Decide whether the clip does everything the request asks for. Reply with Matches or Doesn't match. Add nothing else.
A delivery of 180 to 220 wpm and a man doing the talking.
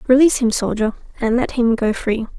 Doesn't match